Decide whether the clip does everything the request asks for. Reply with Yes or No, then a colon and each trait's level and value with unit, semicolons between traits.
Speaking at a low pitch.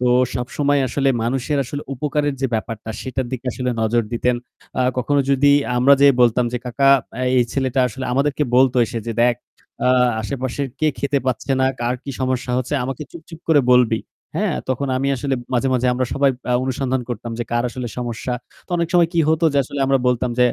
Yes: low, 130 Hz